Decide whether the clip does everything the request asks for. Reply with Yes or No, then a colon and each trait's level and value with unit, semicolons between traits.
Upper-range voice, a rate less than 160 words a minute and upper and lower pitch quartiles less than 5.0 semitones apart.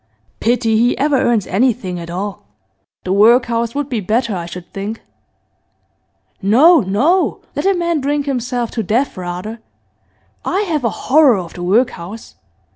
No: high, 230 Hz; average, 150 wpm; wide, 5.6 semitones